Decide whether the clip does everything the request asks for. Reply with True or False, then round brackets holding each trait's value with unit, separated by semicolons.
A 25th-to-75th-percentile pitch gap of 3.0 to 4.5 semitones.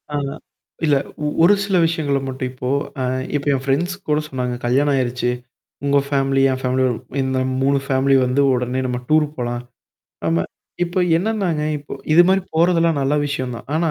True (3.6 semitones)